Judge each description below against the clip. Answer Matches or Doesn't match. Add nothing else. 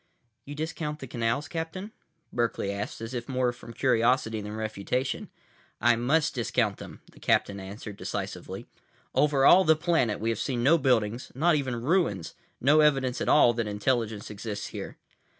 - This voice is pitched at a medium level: Doesn't match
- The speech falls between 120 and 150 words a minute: Doesn't match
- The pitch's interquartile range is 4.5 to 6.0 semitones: Matches